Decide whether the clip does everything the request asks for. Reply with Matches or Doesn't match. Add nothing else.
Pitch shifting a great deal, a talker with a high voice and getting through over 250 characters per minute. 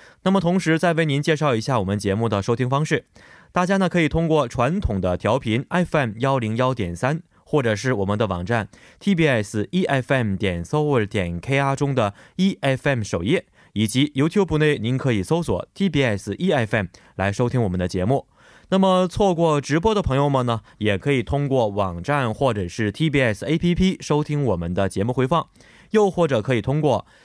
Doesn't match